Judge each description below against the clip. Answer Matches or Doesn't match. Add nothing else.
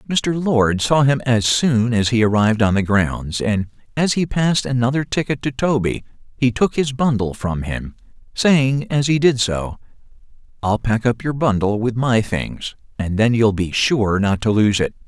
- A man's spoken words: Matches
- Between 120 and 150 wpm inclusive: Doesn't match